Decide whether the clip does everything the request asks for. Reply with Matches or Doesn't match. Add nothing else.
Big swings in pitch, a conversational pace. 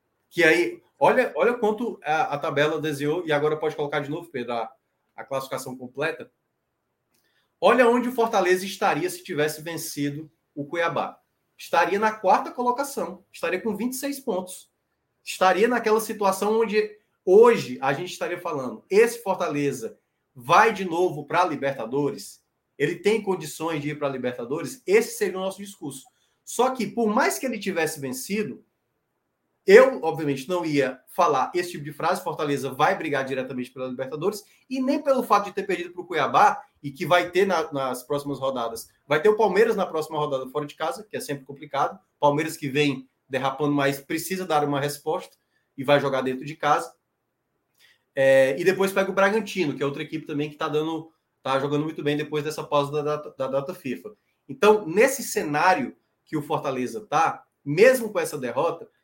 Matches